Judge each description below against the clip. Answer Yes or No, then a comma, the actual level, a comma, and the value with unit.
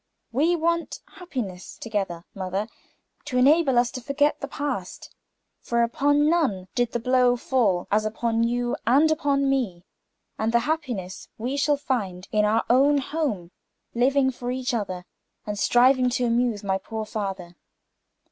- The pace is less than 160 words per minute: Yes, average, 150 wpm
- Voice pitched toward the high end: Yes, high, 245 Hz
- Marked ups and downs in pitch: No, average, 4.9 semitones